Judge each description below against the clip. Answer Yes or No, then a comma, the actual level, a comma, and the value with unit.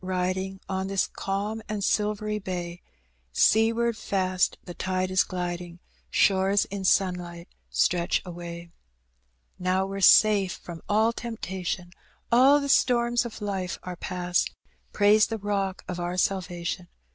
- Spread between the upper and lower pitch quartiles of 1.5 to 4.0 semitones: Yes, average, 2.8 semitones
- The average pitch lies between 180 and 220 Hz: Yes, high, 190 Hz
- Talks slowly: Yes, slow, 130 wpm